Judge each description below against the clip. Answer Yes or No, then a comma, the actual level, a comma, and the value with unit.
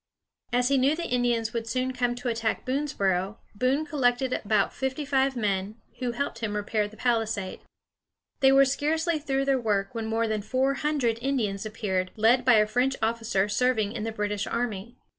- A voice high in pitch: Yes, high, 235 Hz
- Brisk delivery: No, average, 185 wpm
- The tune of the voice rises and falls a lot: No, average, 3.7 semitones